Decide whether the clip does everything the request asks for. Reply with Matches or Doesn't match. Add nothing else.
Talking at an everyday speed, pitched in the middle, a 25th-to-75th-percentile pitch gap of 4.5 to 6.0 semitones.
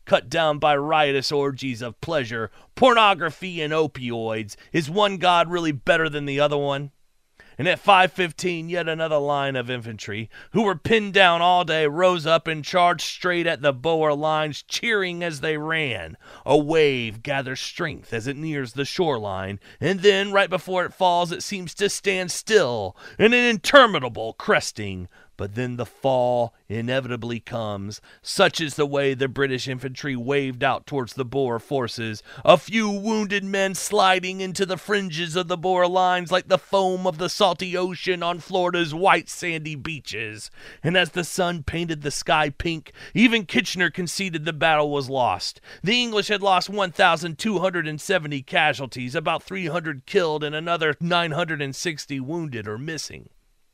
Matches